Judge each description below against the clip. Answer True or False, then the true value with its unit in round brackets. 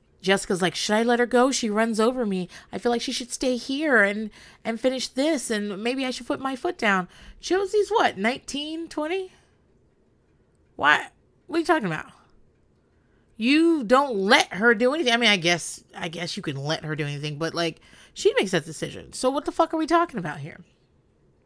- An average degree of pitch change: False (7.7 semitones)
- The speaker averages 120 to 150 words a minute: False (205 wpm)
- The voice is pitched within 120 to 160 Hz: False (240 Hz)